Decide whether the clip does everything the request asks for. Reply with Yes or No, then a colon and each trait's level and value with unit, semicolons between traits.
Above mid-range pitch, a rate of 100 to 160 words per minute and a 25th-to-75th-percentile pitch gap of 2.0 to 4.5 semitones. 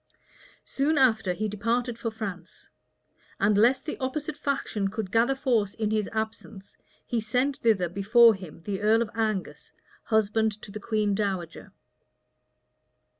Yes: high, 220 Hz; average, 140 wpm; average, 2.8 semitones